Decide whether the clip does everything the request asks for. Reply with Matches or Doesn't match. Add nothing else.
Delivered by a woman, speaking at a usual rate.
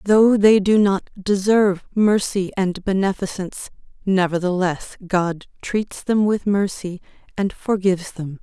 Doesn't match